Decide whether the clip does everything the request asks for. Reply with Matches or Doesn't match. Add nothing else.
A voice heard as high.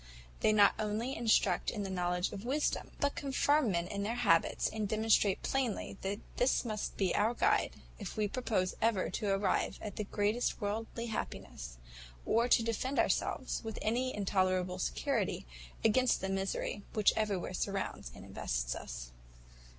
Matches